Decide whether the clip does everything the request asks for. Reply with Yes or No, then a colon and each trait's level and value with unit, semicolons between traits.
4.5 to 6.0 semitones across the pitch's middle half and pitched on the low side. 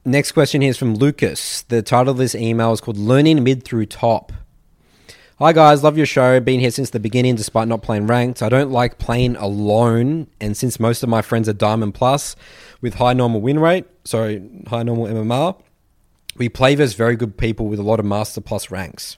No: average, 2.9 semitones; low, 120 Hz